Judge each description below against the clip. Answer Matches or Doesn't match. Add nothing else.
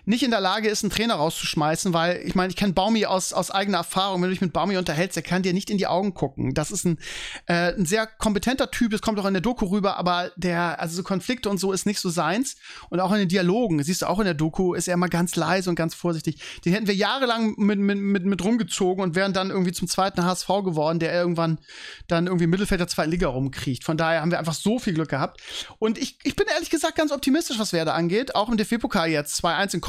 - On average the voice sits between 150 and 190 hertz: Matches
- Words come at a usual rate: Doesn't match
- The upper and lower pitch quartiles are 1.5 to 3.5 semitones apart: Matches